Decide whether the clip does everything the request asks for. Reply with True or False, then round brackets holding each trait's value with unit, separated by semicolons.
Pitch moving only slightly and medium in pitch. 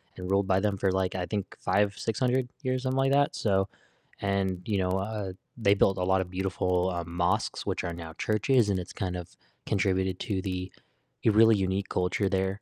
False (2.1 semitones; 95 Hz)